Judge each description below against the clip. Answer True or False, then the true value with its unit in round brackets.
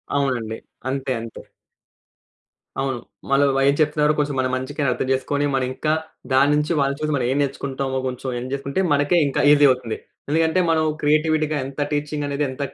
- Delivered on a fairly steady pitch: True (2.0 semitones)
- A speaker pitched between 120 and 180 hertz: True (140 Hz)